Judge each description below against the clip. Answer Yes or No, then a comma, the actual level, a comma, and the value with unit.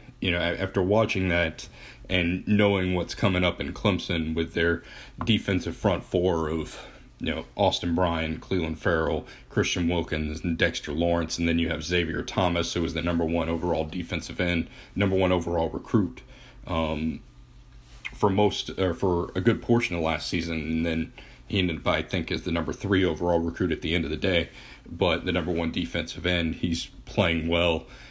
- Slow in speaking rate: No, average, 185 wpm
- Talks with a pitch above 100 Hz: No, very low, 85 Hz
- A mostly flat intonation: Yes, narrow, 2.1 semitones